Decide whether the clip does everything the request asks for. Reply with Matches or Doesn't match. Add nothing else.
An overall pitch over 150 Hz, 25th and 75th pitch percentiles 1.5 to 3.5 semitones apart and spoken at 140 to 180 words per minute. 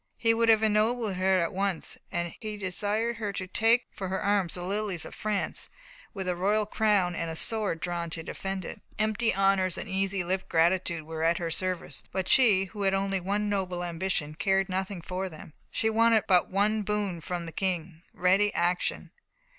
Doesn't match